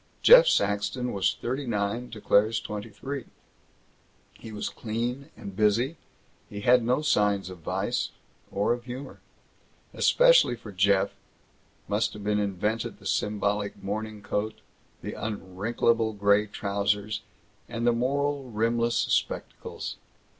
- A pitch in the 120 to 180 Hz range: No, low, 110 Hz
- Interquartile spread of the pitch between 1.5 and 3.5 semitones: Yes, average, 2.9 semitones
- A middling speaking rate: No, slow, 125 wpm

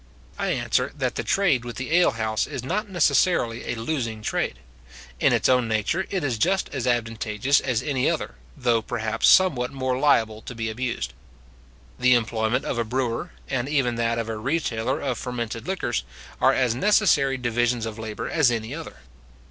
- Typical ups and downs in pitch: Yes, average, 3.2 semitones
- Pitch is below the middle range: Yes, low, 120 Hz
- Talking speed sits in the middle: Yes, average, 175 wpm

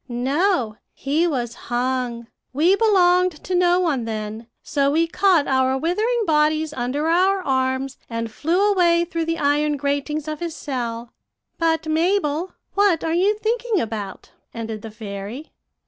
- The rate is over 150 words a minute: No, average, 145 wpm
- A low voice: No, very high, 300 Hz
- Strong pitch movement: Yes, wide, 5.9 semitones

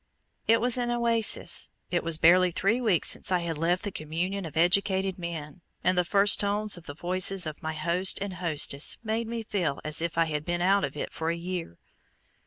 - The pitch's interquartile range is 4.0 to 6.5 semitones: No, average, 3.4 semitones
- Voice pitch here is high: No, medium, 180 Hz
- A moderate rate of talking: No, fast, 210 wpm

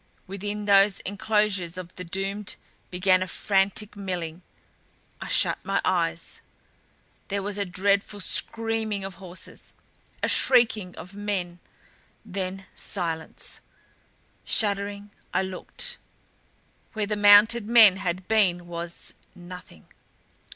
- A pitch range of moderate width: No, narrow, 2.2 semitones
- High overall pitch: Yes, high, 195 Hz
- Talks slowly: Yes, slow, 110 wpm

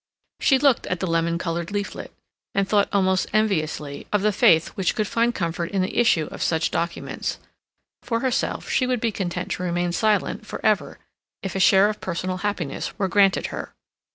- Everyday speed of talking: Yes, average, 185 wpm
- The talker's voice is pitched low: No, high, 190 Hz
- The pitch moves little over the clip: No, average, 3.7 semitones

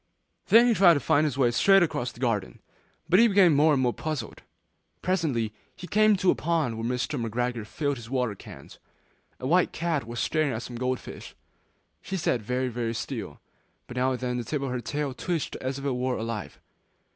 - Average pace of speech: No, fast, 210 wpm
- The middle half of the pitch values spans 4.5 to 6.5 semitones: Yes, average, 4.8 semitones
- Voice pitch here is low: Yes, low, 130 Hz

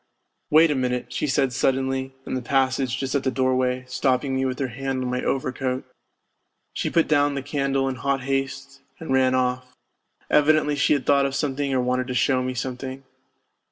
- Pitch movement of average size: No, narrow, 1.3 semitones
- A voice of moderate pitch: No, low, 130 Hz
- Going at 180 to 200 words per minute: Yes, average, 195 wpm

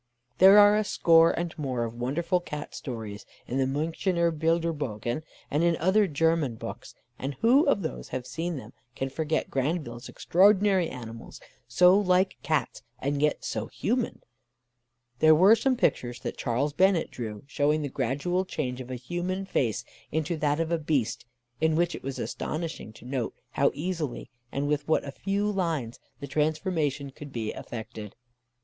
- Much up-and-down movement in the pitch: No, average, 5.0 semitones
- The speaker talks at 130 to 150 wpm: No, average, 170 wpm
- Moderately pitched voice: Yes, medium, 155 Hz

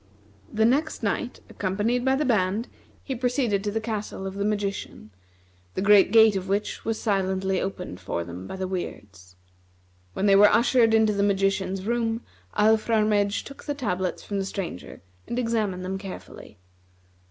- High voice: Yes, high, 205 Hz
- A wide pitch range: No, average, 2.9 semitones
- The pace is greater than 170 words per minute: No, average, 165 wpm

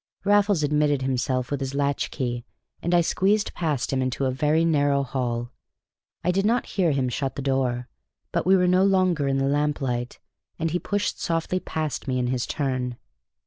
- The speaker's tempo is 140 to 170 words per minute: No, average, 185 wpm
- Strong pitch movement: No, average, 4.8 semitones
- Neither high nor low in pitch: Yes, medium, 145 Hz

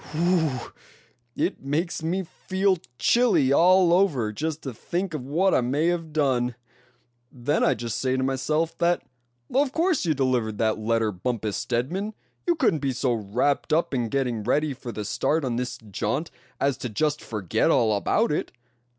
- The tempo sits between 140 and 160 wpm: No, average, 170 wpm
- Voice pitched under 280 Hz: Yes, medium, 140 Hz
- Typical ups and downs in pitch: No, wide, 6.0 semitones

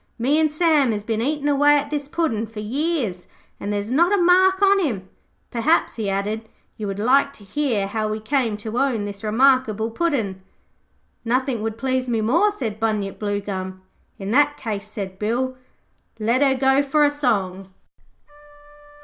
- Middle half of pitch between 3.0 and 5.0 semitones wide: No, wide, 5.5 semitones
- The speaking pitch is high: Yes, high, 235 Hz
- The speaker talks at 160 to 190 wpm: Yes, average, 170 wpm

